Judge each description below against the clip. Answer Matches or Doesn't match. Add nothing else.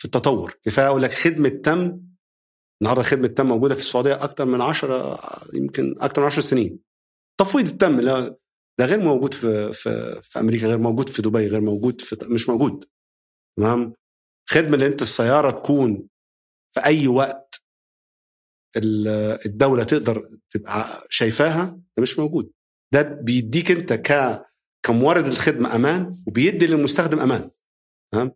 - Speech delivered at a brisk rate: Matches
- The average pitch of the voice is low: Matches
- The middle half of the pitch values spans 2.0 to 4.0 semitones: Doesn't match